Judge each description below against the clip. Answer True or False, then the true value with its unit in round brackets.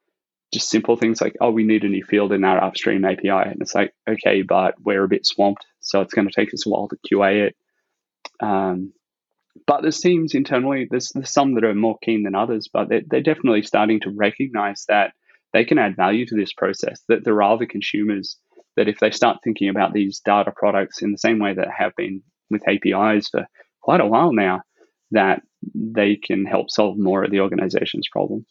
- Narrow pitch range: True (2.3 semitones)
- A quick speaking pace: True (215 wpm)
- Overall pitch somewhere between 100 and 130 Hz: True (105 Hz)